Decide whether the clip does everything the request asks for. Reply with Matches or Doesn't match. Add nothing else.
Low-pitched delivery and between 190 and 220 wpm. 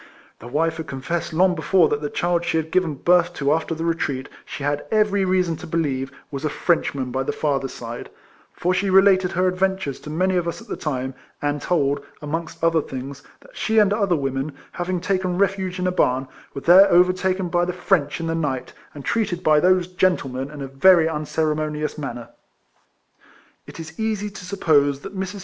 Doesn't match